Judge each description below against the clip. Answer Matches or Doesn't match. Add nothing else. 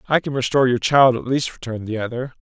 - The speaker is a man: Matches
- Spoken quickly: Matches